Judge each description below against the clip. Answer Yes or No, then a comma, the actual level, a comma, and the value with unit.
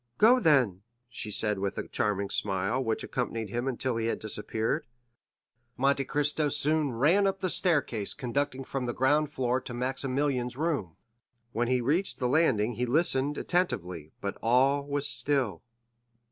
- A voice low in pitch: Yes, low, 130 Hz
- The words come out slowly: No, average, 155 wpm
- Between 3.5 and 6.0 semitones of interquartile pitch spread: Yes, average, 4.3 semitones